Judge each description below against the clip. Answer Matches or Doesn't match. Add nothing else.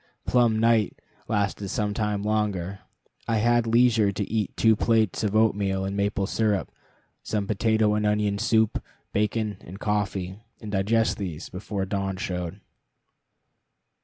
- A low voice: Matches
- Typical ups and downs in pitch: Doesn't match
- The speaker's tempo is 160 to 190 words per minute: Doesn't match